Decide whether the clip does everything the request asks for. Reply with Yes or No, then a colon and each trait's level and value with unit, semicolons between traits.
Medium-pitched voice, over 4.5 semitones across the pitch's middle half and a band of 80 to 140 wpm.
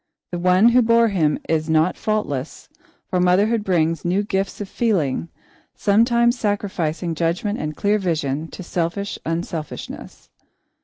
No: medium, 180 Hz; average, 4.2 semitones; slow, 135 wpm